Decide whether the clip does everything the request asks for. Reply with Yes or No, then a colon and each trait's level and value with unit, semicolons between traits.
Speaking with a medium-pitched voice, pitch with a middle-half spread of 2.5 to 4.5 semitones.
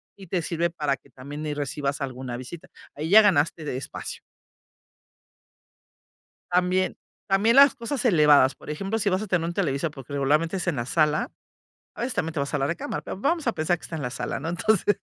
No: medium, 165 Hz; average, 5.1 semitones